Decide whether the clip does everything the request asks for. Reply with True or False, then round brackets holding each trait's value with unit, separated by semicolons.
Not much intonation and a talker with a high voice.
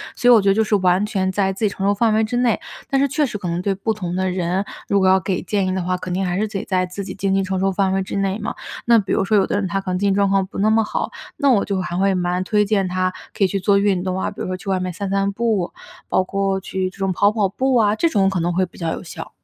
True (2.0 semitones; 195 Hz)